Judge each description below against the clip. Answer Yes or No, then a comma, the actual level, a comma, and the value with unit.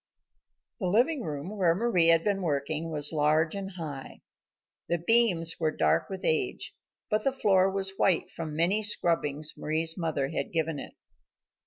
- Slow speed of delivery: No, average, 165 wpm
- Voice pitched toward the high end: No, medium, 165 Hz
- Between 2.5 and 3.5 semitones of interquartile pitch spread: No, average, 3.9 semitones